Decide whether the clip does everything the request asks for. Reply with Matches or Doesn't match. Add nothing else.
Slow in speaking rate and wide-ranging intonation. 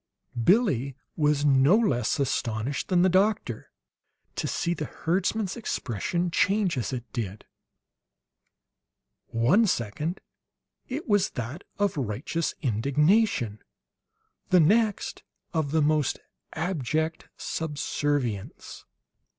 Matches